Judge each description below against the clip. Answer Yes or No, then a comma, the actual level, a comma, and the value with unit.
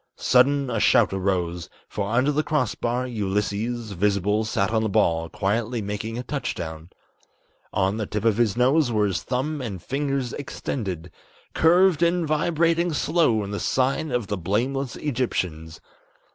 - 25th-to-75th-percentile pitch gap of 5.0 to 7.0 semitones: Yes, wide, 5.6 semitones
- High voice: No, low, 115 Hz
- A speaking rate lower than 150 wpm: No, average, 155 wpm